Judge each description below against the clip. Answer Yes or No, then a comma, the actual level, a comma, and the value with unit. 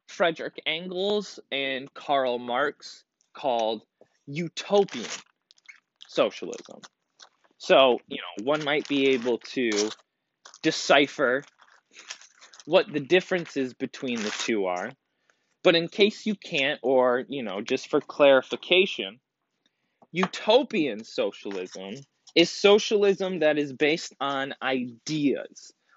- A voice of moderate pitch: Yes, medium, 145 Hz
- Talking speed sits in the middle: No, slow, 100 wpm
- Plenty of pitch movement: No, average, 5.0 semitones